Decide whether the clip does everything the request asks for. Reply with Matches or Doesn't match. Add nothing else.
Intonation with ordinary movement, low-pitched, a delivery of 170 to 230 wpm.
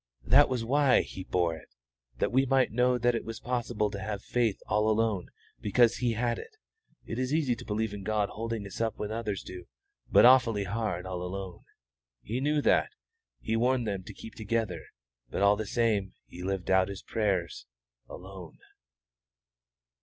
Matches